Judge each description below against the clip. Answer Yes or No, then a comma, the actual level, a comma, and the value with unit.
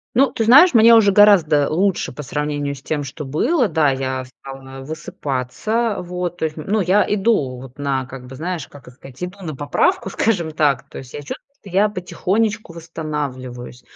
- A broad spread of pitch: Yes, wide, 6.8 semitones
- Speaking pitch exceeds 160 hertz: No, medium, 155 Hz